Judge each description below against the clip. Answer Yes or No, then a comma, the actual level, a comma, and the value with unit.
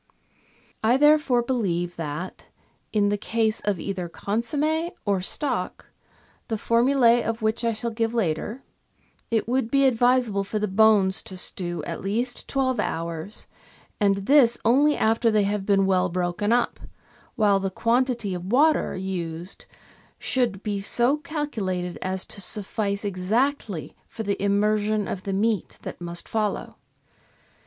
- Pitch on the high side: Yes, high, 215 Hz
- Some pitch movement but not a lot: Yes, average, 3.8 semitones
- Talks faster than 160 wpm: No, average, 145 wpm